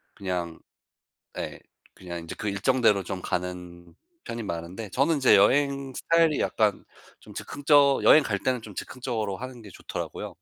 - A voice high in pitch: No, low, 110 Hz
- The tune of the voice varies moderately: No, wide, 6.4 semitones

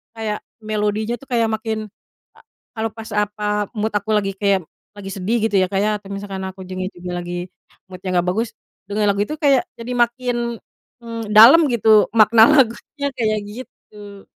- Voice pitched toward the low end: No, high, 215 Hz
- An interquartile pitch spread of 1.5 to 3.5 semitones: Yes, narrow, 2.4 semitones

